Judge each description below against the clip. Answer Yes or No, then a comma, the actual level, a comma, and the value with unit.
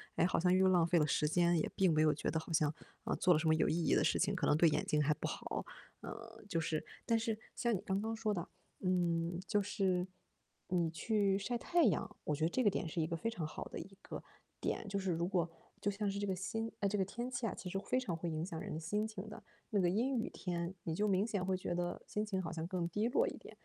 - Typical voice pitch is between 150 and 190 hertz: Yes, medium, 185 Hz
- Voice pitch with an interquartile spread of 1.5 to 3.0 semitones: No, average, 3.8 semitones